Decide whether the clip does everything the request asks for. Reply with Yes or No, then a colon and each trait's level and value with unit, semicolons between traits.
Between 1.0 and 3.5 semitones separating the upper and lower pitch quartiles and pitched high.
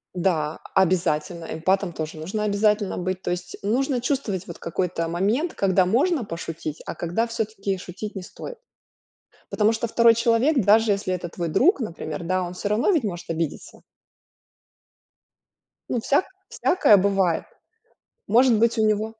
No: average, 4.5 semitones; high, 200 Hz